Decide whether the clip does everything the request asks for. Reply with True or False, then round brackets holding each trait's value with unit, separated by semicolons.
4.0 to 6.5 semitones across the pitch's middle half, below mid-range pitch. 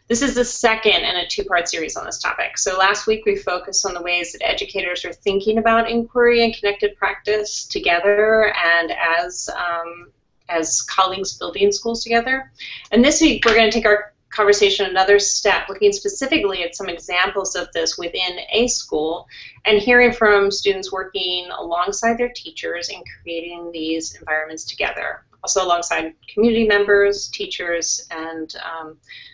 False (4.3 semitones; 200 Hz)